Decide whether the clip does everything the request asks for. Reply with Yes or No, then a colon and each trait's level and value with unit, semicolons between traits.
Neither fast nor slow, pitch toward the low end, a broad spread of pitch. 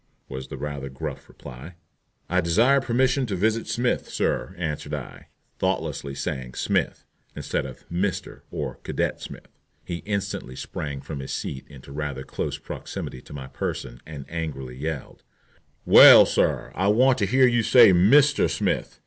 Yes: average, 155 wpm; very low, 85 Hz; wide, 8.3 semitones